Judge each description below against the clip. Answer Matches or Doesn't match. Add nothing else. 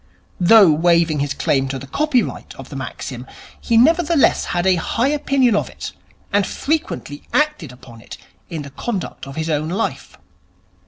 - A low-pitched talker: Doesn't match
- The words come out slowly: Doesn't match